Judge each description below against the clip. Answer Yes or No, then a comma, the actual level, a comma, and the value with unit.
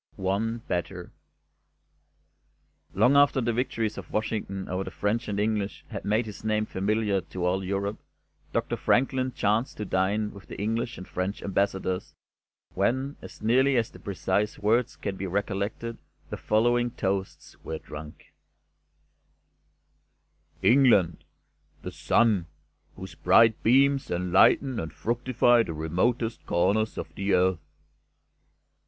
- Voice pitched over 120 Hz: No, low, 105 Hz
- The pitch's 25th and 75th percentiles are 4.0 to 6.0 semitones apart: No, average, 3.5 semitones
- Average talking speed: No, slow, 130 wpm